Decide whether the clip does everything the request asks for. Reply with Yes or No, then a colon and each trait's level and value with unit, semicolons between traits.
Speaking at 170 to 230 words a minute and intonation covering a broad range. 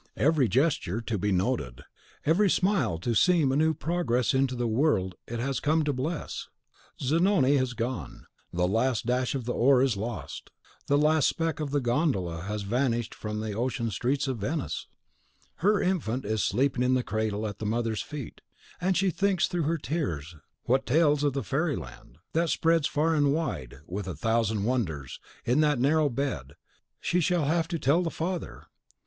Yes: average, 180 wpm; wide, 6.0 semitones